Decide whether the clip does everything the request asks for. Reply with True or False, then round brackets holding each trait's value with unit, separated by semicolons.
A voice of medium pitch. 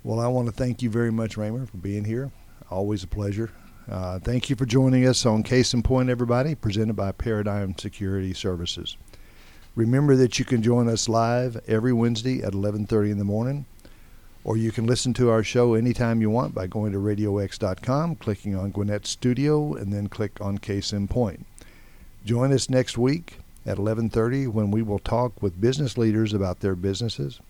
False (110 Hz)